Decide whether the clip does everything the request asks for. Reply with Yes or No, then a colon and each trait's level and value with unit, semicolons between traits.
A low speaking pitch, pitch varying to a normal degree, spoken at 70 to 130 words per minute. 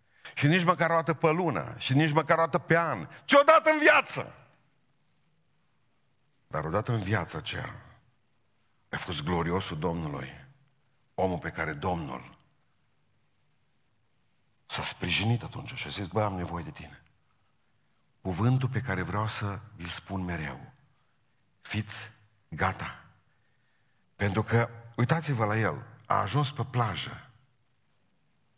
No: low, 120 Hz; wide, 5.9 semitones; average, 125 wpm